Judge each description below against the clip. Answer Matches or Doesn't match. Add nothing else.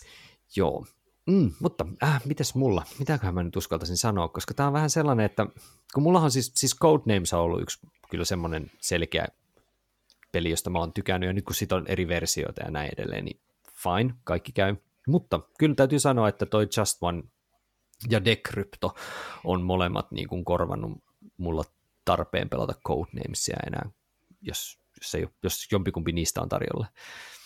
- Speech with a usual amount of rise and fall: Doesn't match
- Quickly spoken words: Matches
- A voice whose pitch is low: Matches